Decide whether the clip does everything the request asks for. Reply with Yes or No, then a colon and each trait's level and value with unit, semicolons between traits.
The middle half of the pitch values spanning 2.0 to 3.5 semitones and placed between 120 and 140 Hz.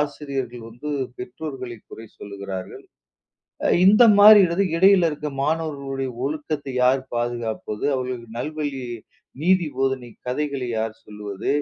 No: average, 4.1 semitones; low, 135 Hz